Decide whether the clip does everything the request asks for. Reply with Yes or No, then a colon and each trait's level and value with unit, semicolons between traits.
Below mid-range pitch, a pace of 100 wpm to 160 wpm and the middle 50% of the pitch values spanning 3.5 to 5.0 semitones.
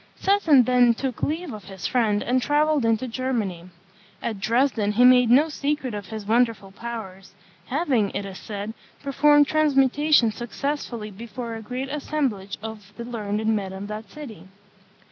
No: high, 235 Hz; average, 155 wpm; average, 4.6 semitones